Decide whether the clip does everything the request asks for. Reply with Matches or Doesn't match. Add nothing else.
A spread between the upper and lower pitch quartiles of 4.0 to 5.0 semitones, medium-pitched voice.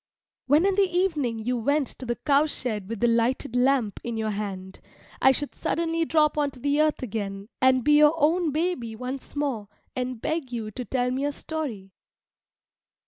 Doesn't match